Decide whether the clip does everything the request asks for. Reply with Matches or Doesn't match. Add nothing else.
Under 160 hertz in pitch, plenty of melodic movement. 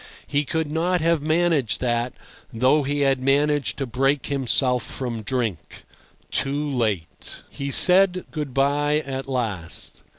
Doesn't match